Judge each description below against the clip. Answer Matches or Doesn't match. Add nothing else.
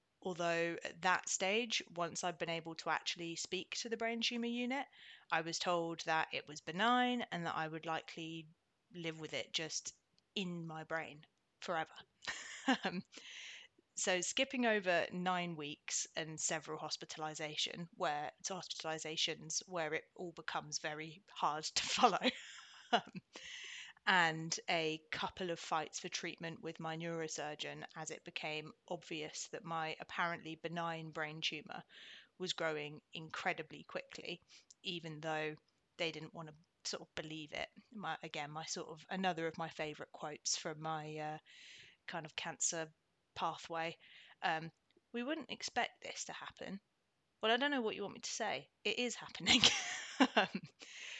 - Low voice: Doesn't match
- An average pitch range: Matches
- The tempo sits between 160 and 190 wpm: Doesn't match